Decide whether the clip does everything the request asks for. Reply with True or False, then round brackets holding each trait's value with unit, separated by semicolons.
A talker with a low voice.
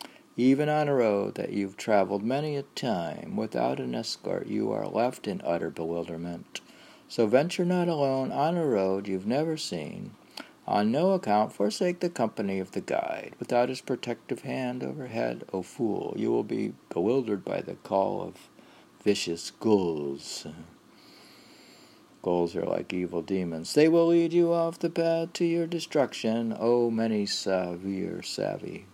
True (115 Hz)